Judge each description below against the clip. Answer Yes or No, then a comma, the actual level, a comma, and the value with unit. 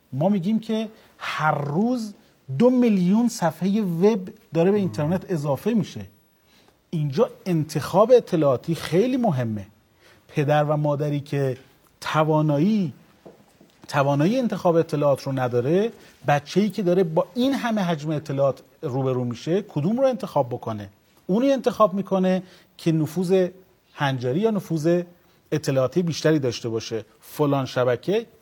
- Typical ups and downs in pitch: No, wide, 5.9 semitones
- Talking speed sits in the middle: Yes, average, 120 wpm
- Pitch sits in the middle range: Yes, medium, 165 Hz